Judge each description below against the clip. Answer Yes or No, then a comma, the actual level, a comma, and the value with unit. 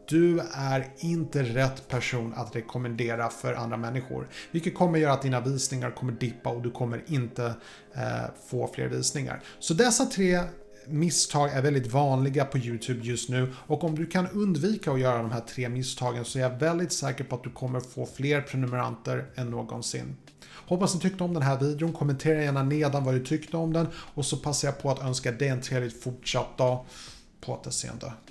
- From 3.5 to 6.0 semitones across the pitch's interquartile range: Yes, average, 3.9 semitones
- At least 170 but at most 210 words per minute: Yes, fast, 195 wpm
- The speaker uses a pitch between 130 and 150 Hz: Yes, low, 135 Hz